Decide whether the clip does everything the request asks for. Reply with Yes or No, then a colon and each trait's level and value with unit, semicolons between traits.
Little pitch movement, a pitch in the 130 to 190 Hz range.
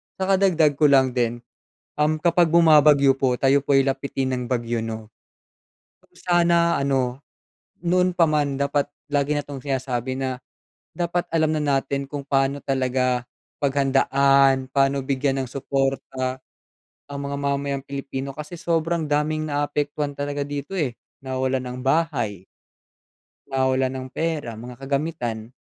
Yes: narrow, 2.2 semitones; medium, 140 Hz